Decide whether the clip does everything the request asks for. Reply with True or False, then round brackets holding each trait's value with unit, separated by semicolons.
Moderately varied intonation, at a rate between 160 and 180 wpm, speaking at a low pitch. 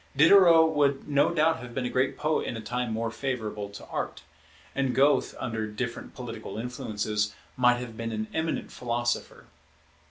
True (3.9 semitones; 165 wpm; 125 Hz)